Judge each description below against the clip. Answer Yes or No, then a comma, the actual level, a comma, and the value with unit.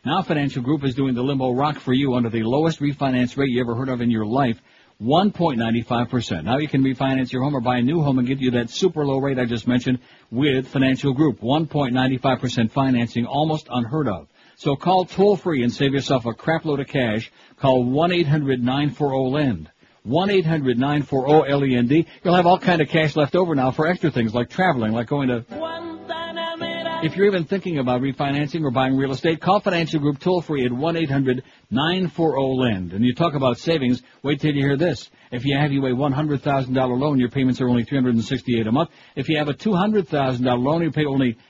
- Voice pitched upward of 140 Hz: No, low, 135 Hz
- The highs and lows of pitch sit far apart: No, average, 3.8 semitones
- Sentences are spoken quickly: No, average, 190 wpm